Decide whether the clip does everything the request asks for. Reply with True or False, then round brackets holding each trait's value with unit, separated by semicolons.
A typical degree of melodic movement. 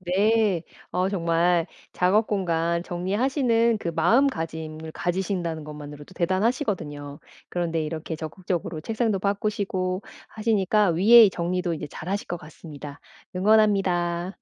True (3.8 semitones)